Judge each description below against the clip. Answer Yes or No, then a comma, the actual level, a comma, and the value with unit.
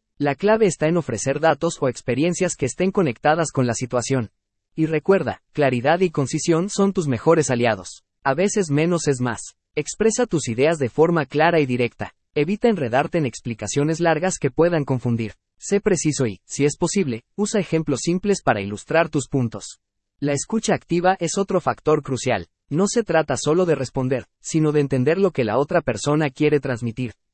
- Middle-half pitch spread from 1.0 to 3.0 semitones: No, average, 5.1 semitones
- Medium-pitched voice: Yes, medium, 150 Hz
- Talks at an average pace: Yes, average, 175 wpm